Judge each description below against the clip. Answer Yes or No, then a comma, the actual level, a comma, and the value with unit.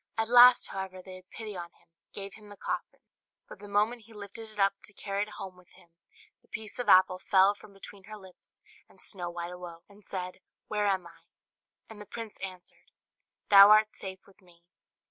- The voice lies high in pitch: Yes, high, 195 Hz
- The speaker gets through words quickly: Yes, fast, 210 wpm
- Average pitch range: No, narrow, 2.3 semitones